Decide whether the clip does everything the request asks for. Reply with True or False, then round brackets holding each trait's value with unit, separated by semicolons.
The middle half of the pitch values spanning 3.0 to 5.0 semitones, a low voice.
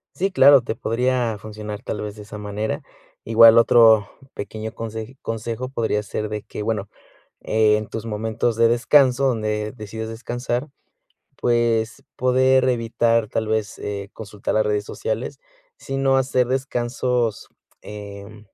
False (2.5 semitones; 115 Hz)